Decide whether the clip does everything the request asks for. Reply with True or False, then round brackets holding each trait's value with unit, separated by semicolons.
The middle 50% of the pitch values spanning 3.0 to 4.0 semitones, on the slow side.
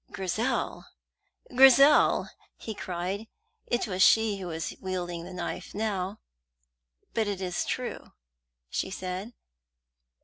True (3.5 semitones; 110 wpm)